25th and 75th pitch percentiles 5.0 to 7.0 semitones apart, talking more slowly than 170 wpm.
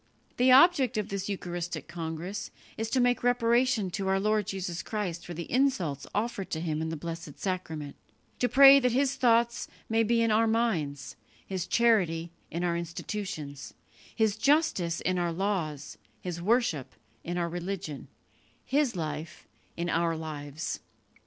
Yes: wide, 5.6 semitones; average, 155 wpm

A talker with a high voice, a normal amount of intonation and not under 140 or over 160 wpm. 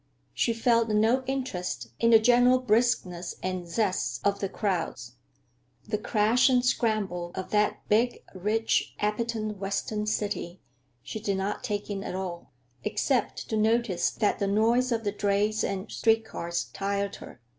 Yes: high, 210 Hz; average, 3.1 semitones; average, 155 wpm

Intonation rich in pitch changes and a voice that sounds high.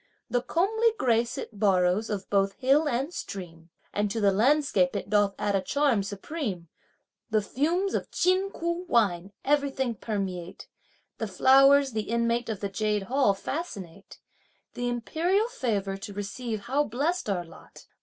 Yes: wide, 6.1 semitones; high, 225 Hz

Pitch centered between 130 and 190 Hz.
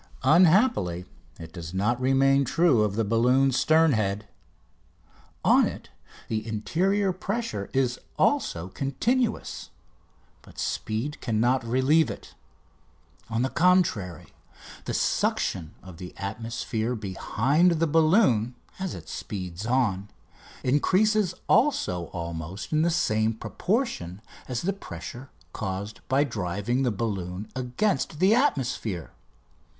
No: low, 120 Hz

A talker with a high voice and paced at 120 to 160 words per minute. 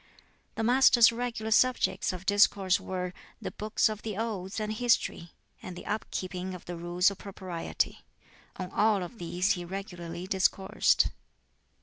Yes: high, 195 Hz; average, 150 wpm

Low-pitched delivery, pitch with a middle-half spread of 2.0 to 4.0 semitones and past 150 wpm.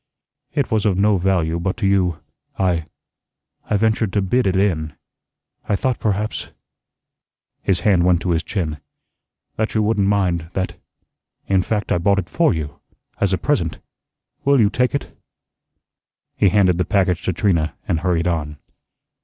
Yes: very low, 95 Hz; average, 3.4 semitones; average, 160 wpm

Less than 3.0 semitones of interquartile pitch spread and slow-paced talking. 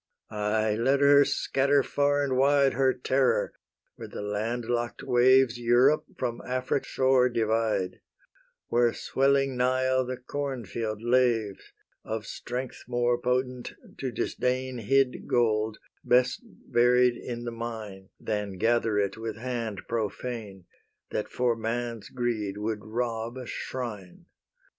Yes: narrow, 2.6 semitones; slow, 130 wpm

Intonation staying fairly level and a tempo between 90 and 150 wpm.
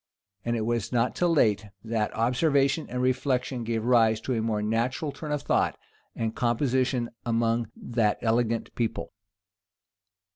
Yes: narrow, 2.2 semitones; average, 145 wpm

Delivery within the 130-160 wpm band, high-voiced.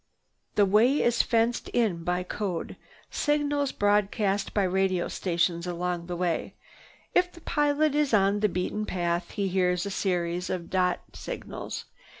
Yes: average, 150 wpm; high, 195 Hz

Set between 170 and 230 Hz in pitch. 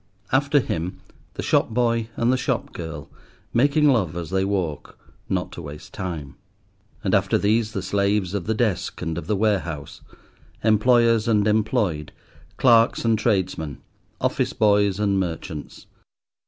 No: low, 105 Hz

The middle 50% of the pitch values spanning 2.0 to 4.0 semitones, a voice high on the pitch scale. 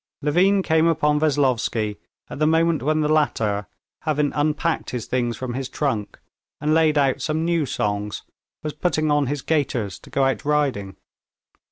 No: average, 3.6 semitones; medium, 145 Hz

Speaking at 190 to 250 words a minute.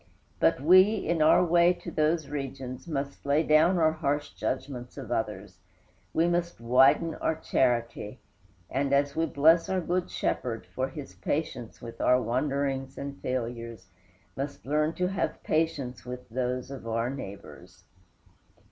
No: average, 145 wpm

